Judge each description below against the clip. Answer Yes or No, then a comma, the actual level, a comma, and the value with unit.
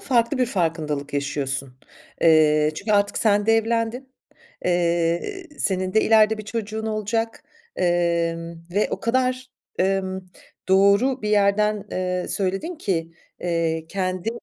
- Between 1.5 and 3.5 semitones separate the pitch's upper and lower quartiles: No, average, 4.6 semitones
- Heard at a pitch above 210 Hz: No, high, 195 Hz